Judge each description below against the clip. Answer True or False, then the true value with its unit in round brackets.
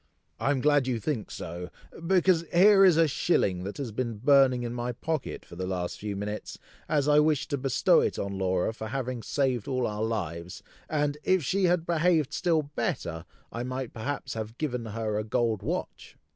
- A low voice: True (125 Hz)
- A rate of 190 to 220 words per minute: True (195 wpm)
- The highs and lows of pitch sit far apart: True (5.9 semitones)